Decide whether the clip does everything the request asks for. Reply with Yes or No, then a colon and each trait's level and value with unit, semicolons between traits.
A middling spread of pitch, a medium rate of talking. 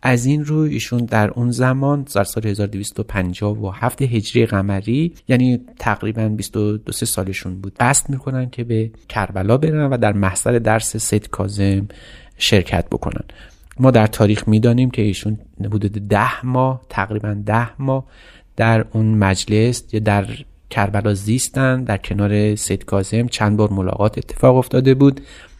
Yes: average, 3.5 semitones; average, 145 wpm